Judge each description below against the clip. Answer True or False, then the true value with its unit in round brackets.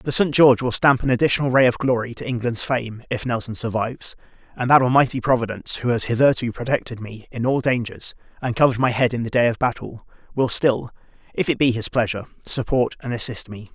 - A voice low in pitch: True (120 Hz)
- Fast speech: True (210 wpm)